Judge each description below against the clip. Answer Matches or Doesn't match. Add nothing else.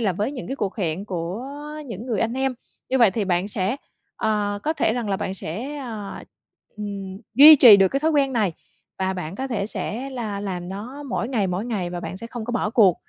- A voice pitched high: Matches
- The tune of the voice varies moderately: Matches